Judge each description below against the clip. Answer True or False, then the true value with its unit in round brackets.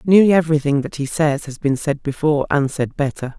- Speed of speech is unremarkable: False (215 wpm)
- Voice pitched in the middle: True (150 Hz)